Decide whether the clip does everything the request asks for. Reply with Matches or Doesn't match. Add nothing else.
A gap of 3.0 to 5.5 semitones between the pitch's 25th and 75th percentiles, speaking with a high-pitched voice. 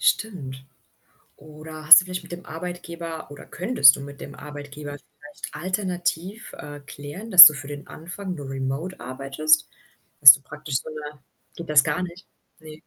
Doesn't match